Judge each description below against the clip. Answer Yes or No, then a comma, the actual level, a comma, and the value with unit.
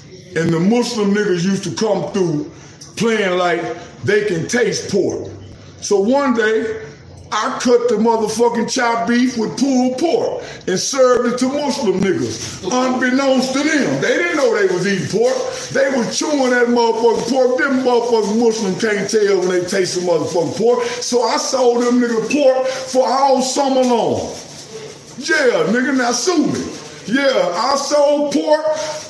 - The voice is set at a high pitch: Yes, high, 240 Hz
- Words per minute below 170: Yes, average, 160 wpm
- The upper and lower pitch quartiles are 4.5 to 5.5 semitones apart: Yes, average, 5.0 semitones